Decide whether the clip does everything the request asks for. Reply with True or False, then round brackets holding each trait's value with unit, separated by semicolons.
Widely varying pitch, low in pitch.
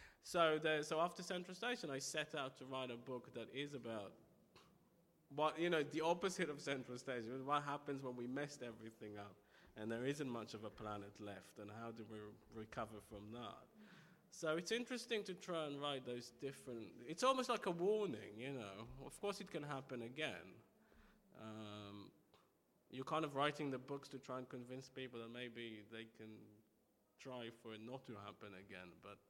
True (5.8 semitones; 130 Hz)